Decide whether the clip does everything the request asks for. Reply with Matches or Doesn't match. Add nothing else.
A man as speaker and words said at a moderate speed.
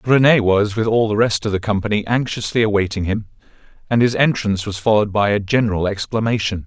Matches